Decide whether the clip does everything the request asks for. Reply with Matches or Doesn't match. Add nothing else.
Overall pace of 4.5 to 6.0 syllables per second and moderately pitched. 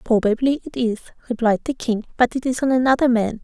Doesn't match